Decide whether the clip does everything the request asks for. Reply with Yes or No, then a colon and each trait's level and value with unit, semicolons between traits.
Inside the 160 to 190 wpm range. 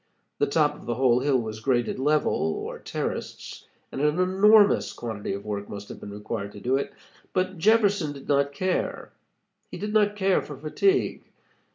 Yes: average, 180 wpm